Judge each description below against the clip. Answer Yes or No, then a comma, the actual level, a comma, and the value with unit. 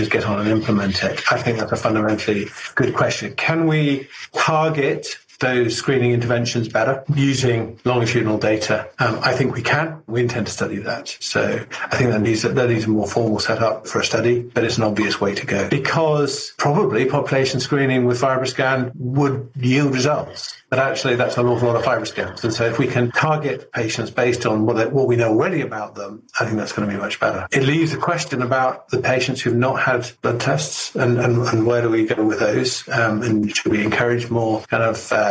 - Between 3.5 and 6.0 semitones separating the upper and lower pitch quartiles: No, average, 3.1 semitones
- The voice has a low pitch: Yes, low, 120 Hz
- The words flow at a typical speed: No, fast, 215 wpm